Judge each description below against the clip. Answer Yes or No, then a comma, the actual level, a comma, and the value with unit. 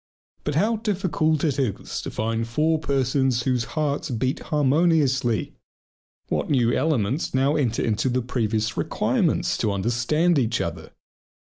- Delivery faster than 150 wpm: No, slow, 135 wpm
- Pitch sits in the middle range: No, low, 130 Hz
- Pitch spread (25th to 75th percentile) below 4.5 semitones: No, average, 4.8 semitones